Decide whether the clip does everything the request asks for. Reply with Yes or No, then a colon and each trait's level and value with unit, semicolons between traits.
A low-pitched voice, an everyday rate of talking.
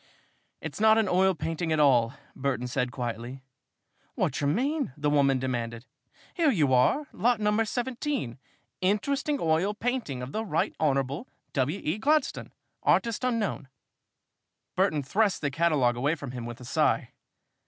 No: medium, 155 Hz; average, 155 wpm